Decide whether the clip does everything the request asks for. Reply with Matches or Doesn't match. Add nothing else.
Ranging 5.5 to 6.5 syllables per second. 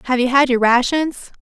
Doesn't match